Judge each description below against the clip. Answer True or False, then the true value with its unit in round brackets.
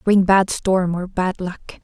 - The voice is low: False (185 Hz)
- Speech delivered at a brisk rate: False (195 wpm)